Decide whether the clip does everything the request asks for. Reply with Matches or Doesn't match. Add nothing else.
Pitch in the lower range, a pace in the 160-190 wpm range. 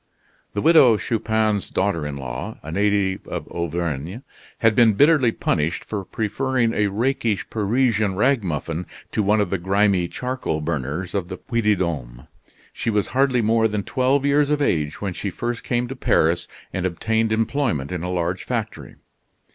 Matches